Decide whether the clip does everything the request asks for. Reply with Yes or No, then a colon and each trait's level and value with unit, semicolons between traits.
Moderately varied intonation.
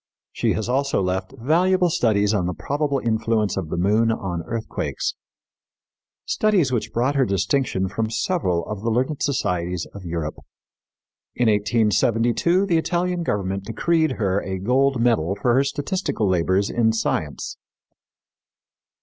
No: wide, 6.2 semitones